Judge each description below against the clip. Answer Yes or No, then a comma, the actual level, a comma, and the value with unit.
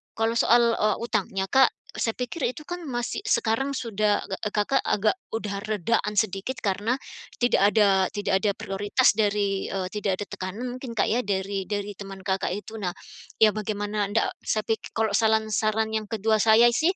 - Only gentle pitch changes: Yes, narrow, 2.1 semitones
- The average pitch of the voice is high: Yes, high, 215 Hz